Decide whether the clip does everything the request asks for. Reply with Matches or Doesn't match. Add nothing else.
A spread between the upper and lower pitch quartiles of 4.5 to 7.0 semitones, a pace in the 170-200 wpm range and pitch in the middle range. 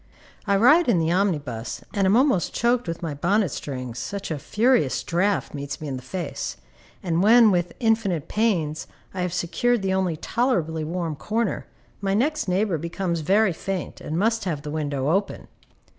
Matches